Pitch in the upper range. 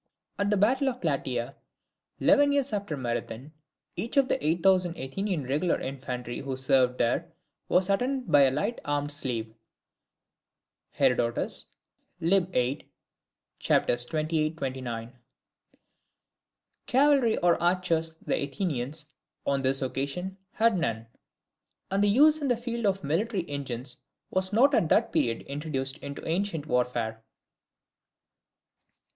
No: medium, 160 Hz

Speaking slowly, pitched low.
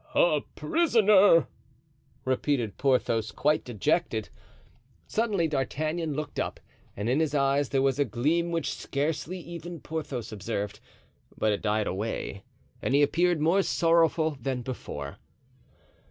No: slow, 125 wpm; medium, 145 Hz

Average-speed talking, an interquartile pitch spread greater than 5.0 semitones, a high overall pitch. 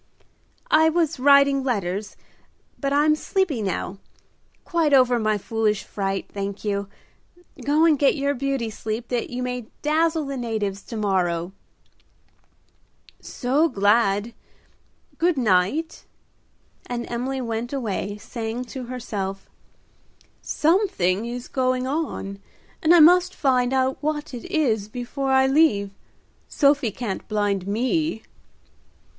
No: slow, 120 wpm; wide, 5.4 semitones; very high, 250 Hz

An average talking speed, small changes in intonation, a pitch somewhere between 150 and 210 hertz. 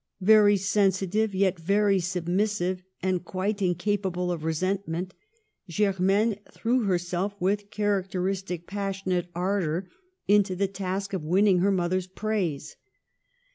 No: slow, 115 wpm; narrow, 2.0 semitones; high, 190 Hz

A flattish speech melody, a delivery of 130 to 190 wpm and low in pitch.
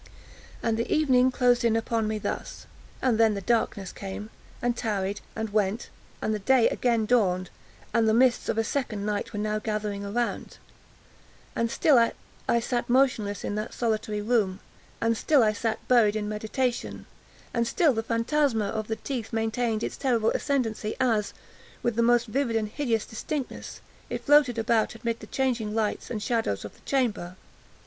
No: narrow, 2.3 semitones; average, 155 wpm; high, 225 Hz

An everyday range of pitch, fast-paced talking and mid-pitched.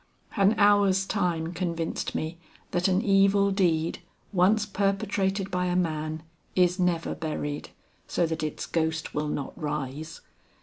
No: average, 3.6 semitones; slow, 135 wpm; medium, 180 Hz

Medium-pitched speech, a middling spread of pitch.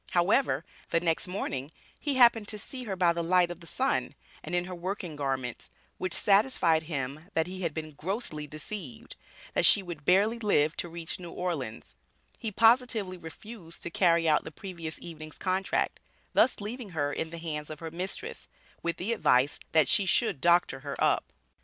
Yes: medium, 175 Hz; average, 4.0 semitones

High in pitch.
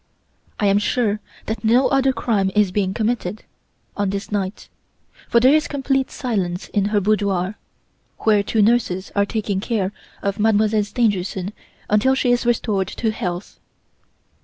Yes: high, 210 Hz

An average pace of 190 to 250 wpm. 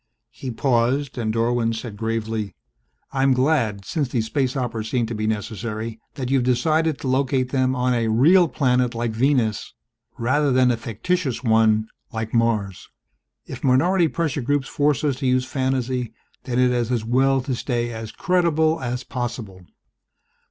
No: average, 165 wpm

